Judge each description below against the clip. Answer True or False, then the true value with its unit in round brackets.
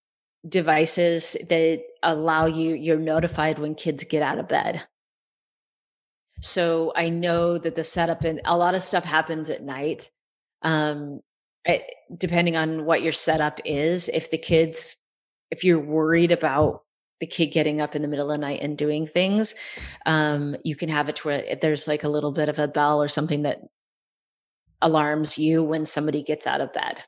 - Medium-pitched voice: True (160 Hz)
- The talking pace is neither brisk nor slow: True (175 wpm)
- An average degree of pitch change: False (1.7 semitones)